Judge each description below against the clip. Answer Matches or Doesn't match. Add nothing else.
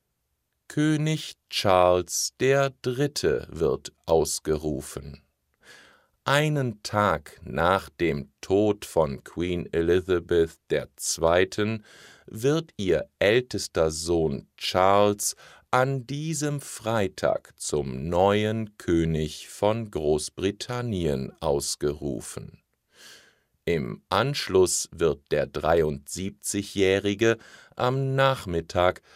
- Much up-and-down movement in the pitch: Matches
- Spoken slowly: Matches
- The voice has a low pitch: Matches